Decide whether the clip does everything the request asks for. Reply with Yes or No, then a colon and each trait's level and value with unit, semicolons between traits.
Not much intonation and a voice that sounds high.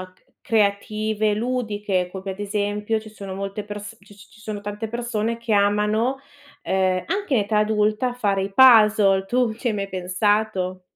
Yes: narrow, 1.9 semitones; high, 210 Hz